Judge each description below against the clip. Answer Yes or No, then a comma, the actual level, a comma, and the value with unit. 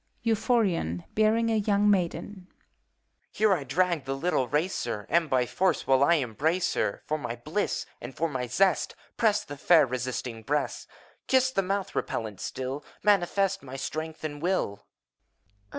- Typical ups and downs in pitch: No, wide, 6.9 semitones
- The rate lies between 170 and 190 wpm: No, average, 155 wpm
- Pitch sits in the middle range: Yes, medium, 160 Hz